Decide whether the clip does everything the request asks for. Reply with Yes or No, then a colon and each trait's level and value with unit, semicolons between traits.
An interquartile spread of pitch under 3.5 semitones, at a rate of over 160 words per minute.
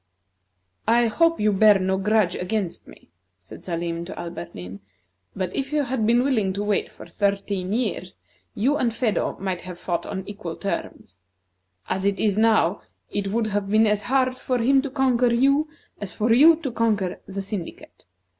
No: average, 4.1 semitones; average, 175 wpm